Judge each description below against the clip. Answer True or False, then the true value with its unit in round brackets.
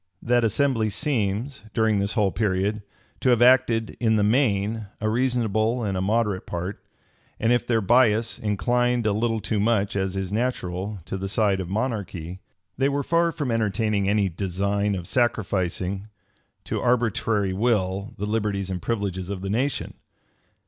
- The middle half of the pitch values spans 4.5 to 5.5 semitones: False (3.3 semitones)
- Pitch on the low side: True (105 Hz)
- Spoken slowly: False (160 wpm)